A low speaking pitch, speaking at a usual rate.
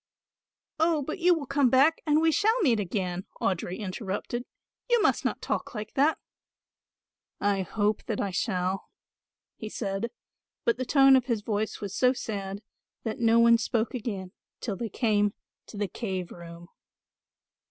No: high, 220 Hz; average, 160 wpm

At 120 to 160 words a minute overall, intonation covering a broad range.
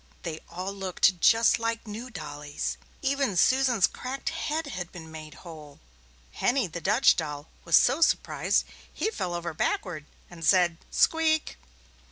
Yes: average, 145 wpm; wide, 7.6 semitones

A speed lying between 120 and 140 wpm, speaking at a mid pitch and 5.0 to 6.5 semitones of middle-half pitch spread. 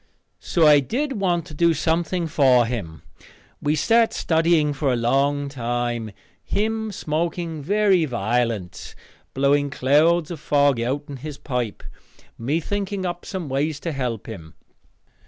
Yes: slow, 135 wpm; medium, 145 Hz; average, 5.3 semitones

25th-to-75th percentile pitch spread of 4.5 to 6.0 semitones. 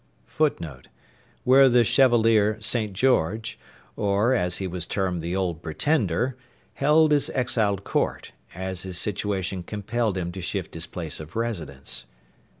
Yes: average, 5.1 semitones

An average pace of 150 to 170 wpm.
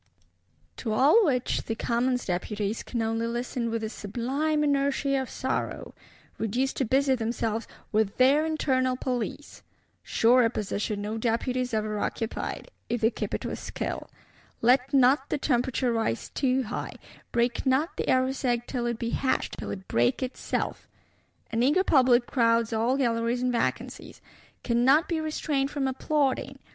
Yes: average, 155 wpm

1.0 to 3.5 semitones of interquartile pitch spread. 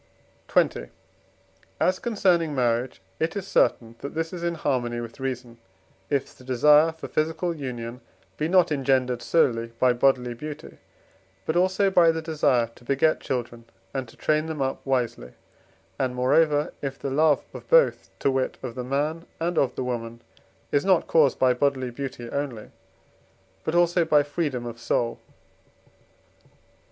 No: average, 4.5 semitones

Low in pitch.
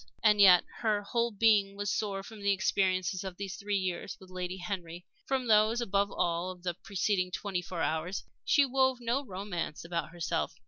No: high, 195 Hz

